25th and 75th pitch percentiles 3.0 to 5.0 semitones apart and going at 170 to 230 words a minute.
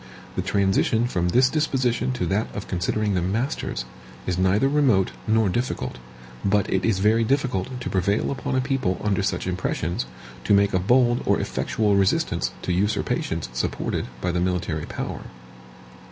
No: average, 4.6 semitones; average, 160 wpm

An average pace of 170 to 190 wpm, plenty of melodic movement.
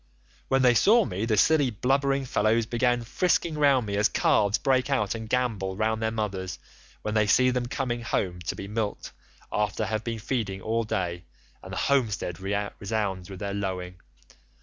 No: average, 180 wpm; average, 4.0 semitones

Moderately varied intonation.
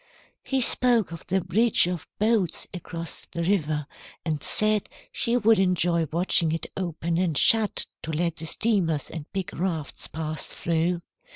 Yes: average, 3.8 semitones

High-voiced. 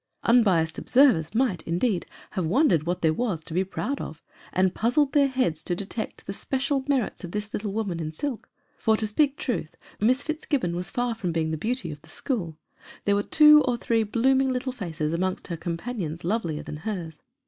Yes: high, 205 Hz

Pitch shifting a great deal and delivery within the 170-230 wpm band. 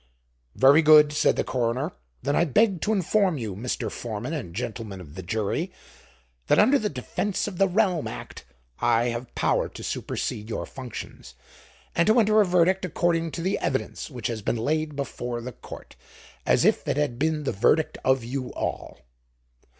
Yes: wide, 6.7 semitones; average, 180 wpm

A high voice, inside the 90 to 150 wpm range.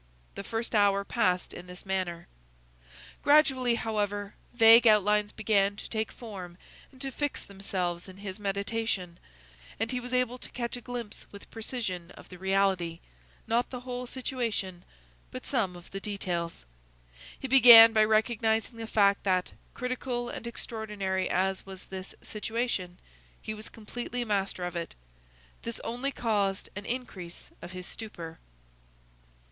Yes: high, 210 Hz; average, 145 wpm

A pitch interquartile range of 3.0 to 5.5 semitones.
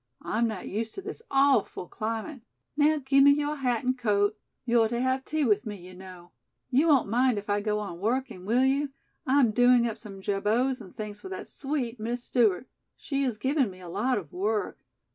Yes: average, 4.4 semitones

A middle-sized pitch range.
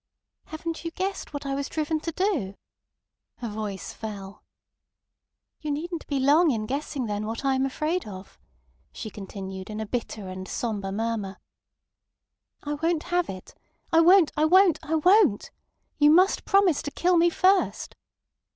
No: wide, 7.7 semitones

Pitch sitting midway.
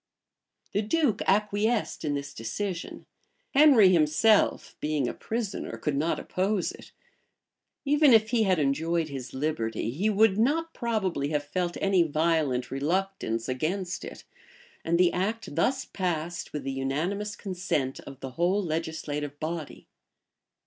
Yes: medium, 175 Hz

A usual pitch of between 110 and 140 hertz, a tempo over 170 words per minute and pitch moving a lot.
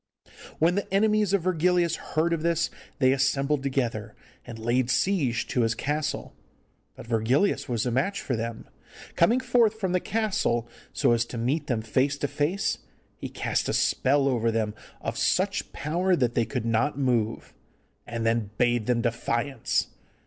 No: low, 135 Hz; average, 165 wpm; wide, 6.4 semitones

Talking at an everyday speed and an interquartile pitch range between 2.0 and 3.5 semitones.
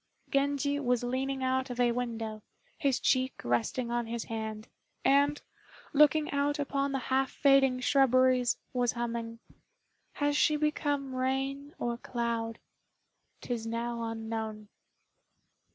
No: slow, 120 wpm; average, 2.9 semitones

